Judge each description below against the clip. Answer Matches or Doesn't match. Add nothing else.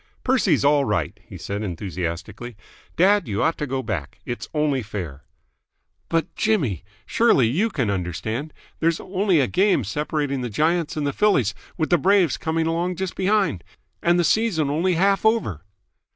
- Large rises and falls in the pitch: Matches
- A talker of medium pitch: Matches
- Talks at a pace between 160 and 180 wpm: Matches